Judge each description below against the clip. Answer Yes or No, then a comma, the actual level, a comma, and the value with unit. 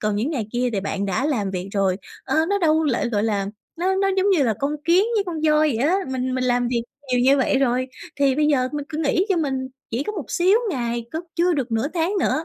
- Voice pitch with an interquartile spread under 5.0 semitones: No, average, 5.3 semitones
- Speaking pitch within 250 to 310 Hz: Yes, very high, 270 Hz